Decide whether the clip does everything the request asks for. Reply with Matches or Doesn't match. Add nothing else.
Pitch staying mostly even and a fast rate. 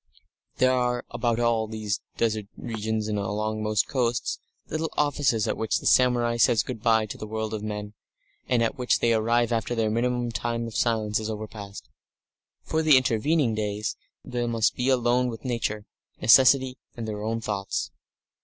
Doesn't match